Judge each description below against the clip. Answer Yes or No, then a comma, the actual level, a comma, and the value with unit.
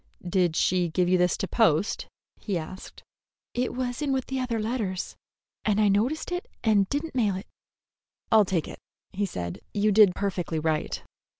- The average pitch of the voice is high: Yes, high, 200 Hz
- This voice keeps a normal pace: Yes, average, 175 wpm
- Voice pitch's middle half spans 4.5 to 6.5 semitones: Yes, average, 4.9 semitones